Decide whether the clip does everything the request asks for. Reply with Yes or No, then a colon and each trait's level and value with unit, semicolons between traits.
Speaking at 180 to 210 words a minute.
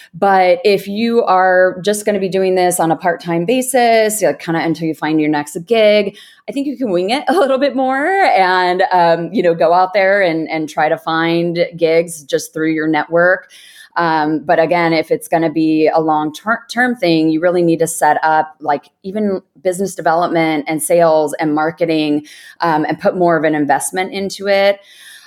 Yes: average, 200 wpm